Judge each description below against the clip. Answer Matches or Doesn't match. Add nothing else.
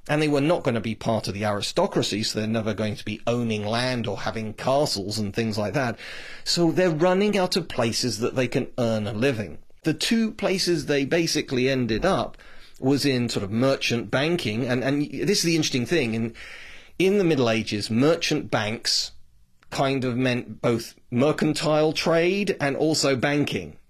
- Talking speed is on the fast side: Doesn't match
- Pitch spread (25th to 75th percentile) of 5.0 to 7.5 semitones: Matches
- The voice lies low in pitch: Matches